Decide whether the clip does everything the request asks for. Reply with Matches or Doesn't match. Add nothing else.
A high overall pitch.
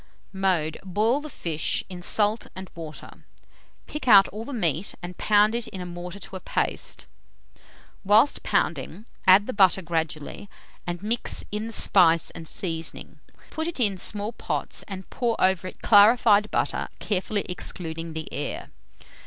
Matches